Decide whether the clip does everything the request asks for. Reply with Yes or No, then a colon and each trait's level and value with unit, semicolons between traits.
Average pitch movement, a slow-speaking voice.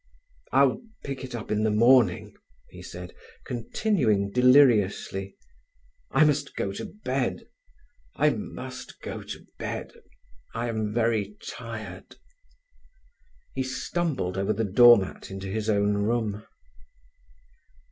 Yes: average, 4.3 semitones; slow, 110 wpm